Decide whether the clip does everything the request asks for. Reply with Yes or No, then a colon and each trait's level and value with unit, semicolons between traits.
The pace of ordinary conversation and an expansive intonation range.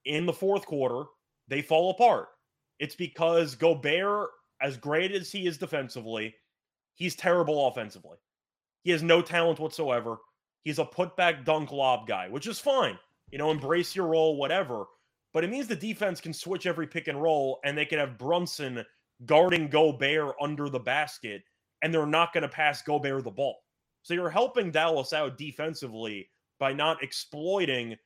No: average, 165 wpm; average, 3.7 semitones